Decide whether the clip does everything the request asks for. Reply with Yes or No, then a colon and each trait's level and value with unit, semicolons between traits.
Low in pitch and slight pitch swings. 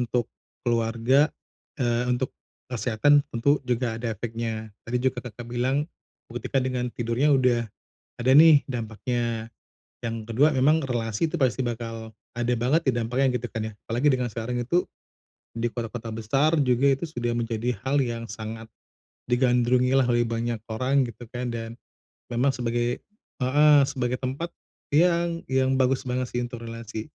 Yes: low, 120 Hz; narrow, 2.2 semitones